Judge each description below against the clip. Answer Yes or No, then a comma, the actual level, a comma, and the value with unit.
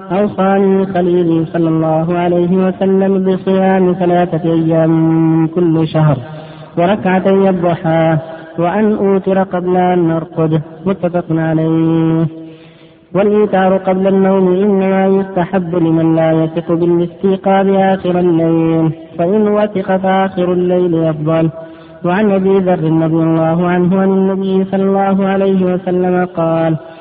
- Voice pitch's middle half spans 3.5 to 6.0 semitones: No, average, 2.8 semitones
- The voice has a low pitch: No, medium, 175 Hz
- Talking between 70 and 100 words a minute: No, average, 110 wpm